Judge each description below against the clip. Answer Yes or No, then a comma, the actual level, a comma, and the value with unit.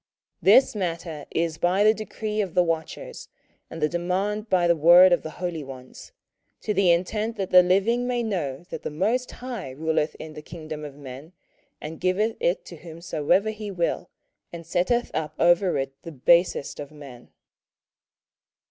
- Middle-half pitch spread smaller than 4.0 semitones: No, average, 4.6 semitones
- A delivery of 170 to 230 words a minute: Yes, average, 175 wpm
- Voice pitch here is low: No, medium, 175 Hz